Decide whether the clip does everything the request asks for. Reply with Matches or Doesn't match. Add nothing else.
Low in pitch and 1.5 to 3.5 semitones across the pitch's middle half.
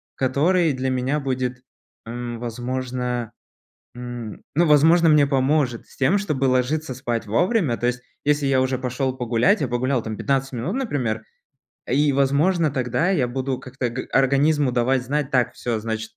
Matches